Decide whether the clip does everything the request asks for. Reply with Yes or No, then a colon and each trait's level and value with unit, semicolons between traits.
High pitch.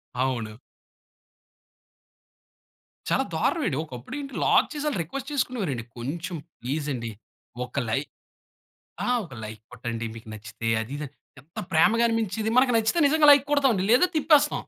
No: medium, 165 Hz